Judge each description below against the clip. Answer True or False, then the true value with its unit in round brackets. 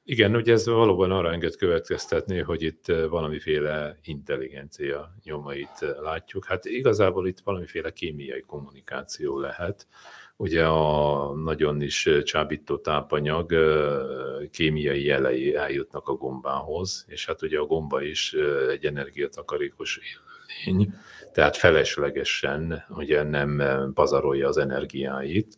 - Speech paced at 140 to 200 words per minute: False (110 wpm)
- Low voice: True (80 Hz)